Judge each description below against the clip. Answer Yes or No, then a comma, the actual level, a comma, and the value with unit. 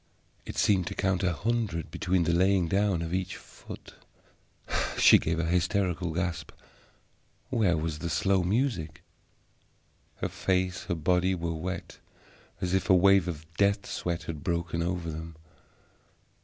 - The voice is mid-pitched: No, very low, 90 Hz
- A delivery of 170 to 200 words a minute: No, average, 145 wpm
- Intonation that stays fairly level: Yes, narrow, 2.3 semitones